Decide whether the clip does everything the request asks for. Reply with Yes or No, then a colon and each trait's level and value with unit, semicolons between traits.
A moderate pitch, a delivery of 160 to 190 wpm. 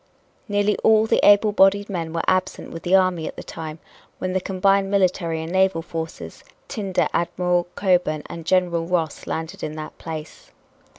Yes: medium, 180 Hz; average, 170 wpm